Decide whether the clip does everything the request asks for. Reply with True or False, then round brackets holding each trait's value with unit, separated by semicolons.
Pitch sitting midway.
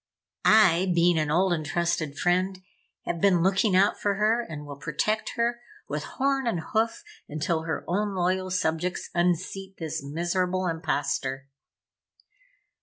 True (180 Hz)